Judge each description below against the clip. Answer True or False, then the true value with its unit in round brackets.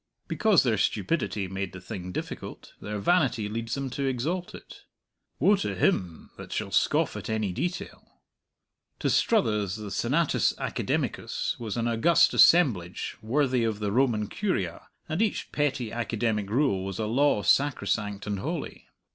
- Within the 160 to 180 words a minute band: False (150 wpm)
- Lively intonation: True (5.8 semitones)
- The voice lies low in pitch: True (115 Hz)